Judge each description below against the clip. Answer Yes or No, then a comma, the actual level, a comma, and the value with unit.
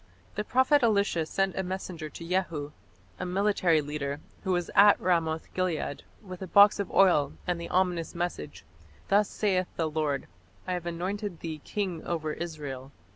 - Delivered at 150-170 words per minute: Yes, average, 165 wpm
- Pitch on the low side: No, medium, 175 Hz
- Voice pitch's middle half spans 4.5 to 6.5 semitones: No, average, 3.4 semitones